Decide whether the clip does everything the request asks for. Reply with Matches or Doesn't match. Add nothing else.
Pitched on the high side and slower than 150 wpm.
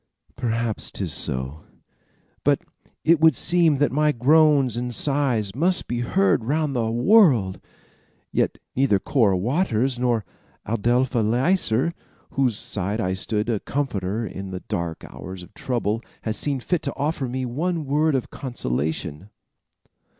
Doesn't match